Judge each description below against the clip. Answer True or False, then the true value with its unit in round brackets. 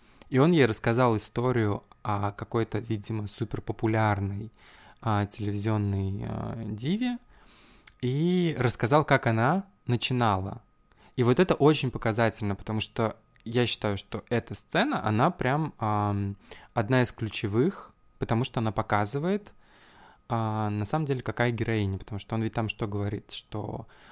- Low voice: True (115 Hz)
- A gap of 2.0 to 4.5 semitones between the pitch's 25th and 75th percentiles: True (3.1 semitones)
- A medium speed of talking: True (135 wpm)